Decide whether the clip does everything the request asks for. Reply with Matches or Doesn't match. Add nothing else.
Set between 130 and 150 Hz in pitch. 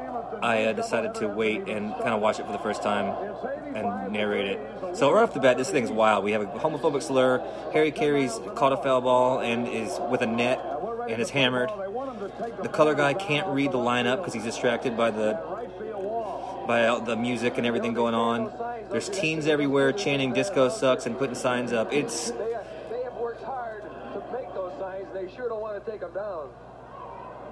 Matches